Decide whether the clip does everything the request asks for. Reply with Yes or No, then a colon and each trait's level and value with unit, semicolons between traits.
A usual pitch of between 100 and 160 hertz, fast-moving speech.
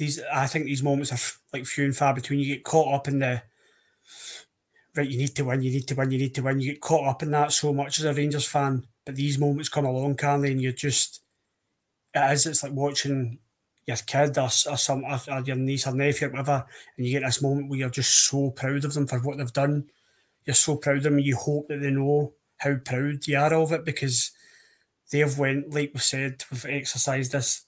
Yes: medium, 140 Hz; fast, 245 wpm